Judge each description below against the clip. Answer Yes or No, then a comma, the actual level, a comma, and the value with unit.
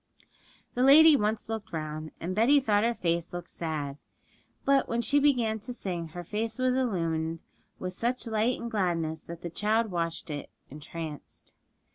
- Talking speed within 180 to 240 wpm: No, average, 165 wpm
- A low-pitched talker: No, high, 205 Hz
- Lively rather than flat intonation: Yes, wide, 6.0 semitones